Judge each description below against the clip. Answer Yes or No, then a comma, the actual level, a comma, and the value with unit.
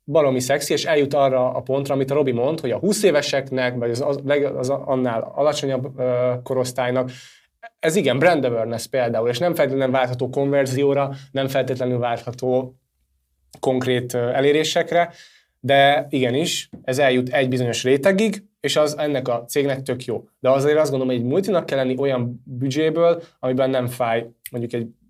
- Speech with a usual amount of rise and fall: No, narrow, 2.3 semitones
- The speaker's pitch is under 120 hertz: No, low, 135 Hz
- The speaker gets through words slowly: No, fast, 155 wpm